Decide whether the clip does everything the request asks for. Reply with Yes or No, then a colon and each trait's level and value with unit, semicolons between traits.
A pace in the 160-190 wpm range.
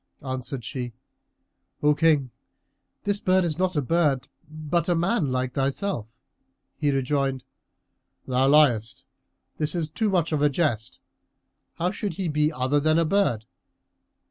No: average, 140 wpm